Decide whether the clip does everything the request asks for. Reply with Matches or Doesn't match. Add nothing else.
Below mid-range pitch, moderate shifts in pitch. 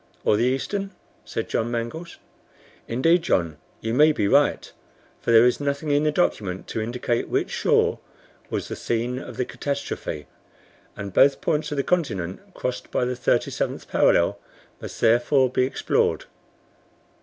Matches